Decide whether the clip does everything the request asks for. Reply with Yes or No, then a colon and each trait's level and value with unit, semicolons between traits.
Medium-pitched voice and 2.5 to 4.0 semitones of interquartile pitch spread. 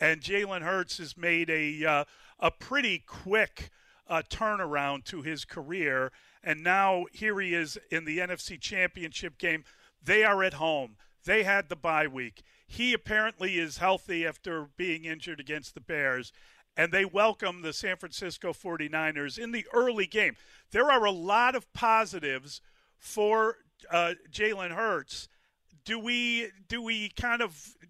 No: medium, 180 Hz; average, 5.1 semitones